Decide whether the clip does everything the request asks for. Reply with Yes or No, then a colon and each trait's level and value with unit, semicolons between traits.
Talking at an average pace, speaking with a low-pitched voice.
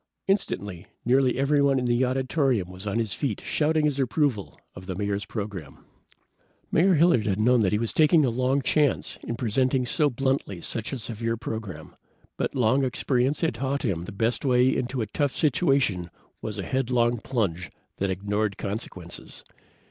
Yes: average, 165 wpm; low, 120 Hz